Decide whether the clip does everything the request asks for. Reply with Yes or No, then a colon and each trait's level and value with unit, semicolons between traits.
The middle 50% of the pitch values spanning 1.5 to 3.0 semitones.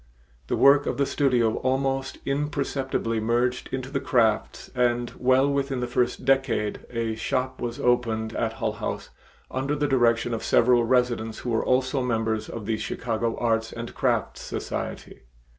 Yes: narrow, 2.6 semitones